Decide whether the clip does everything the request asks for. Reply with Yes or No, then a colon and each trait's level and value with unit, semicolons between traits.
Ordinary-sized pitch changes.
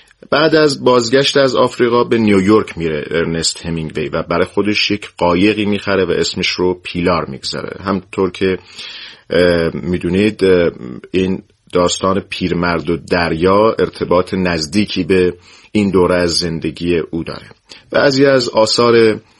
Yes: average, 3.6 semitones